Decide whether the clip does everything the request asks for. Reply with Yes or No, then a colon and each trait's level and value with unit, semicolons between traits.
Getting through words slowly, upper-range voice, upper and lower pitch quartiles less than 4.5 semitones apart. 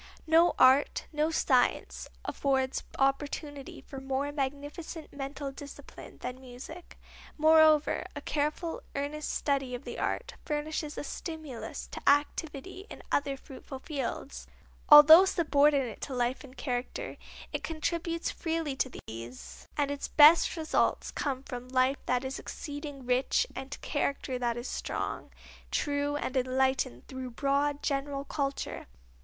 Yes: slow, 130 wpm; very high, 280 Hz; narrow, 2.5 semitones